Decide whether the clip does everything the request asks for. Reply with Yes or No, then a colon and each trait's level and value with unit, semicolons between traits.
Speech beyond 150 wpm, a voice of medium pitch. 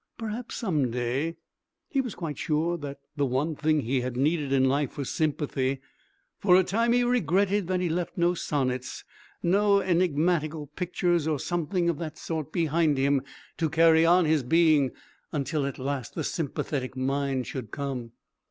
Yes: average, 165 wpm; medium, 155 Hz